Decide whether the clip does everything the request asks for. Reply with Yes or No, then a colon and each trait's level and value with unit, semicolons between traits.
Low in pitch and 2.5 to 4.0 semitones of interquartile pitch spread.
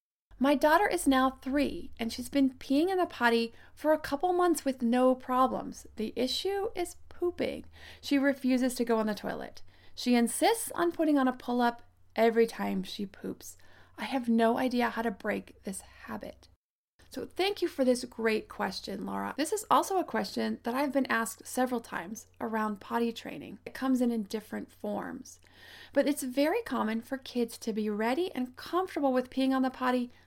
No: very high, 255 Hz; average, 3.6 semitones